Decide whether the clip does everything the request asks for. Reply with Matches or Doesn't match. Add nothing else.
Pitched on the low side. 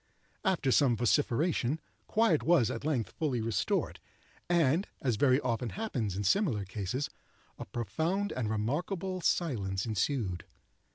Matches